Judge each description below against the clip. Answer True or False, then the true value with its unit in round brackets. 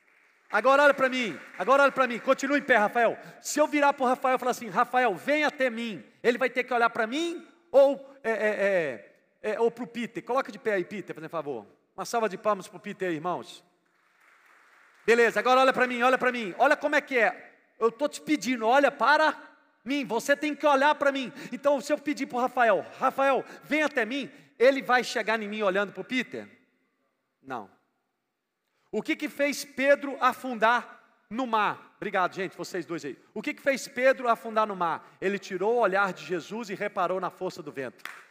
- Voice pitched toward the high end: True (245 Hz)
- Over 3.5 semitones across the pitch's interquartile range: True (4.8 semitones)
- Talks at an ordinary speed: False (210 wpm)